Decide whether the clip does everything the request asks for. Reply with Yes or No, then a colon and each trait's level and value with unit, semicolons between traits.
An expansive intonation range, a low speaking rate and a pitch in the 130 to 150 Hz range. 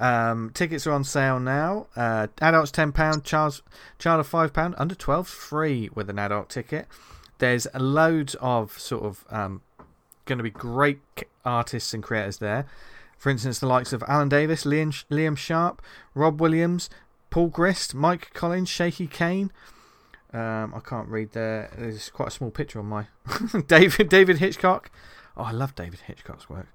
No: wide, 5.9 semitones; average, 170 wpm; medium, 140 Hz